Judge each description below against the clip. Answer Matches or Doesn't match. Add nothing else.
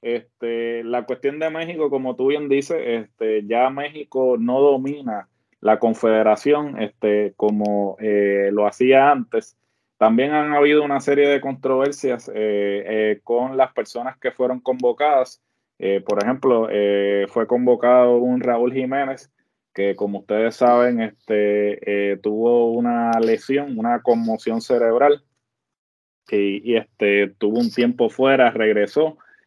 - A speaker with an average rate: Matches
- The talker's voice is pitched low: Matches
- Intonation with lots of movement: Doesn't match